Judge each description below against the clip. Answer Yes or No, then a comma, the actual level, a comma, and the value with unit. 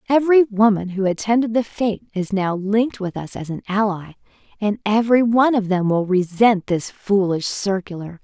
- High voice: Yes, high, 205 Hz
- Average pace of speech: Yes, average, 175 wpm